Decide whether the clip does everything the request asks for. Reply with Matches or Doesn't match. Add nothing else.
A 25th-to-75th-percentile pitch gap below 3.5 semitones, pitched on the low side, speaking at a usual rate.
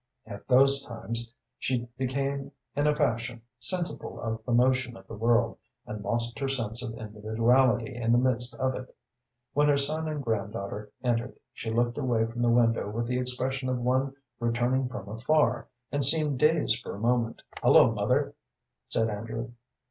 Matches